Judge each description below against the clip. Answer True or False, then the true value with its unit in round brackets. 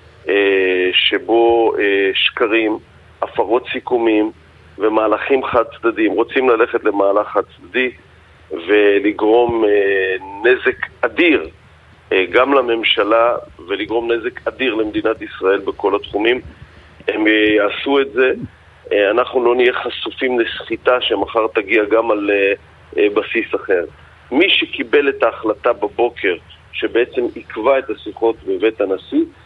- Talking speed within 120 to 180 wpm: False (100 wpm)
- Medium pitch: False (120 Hz)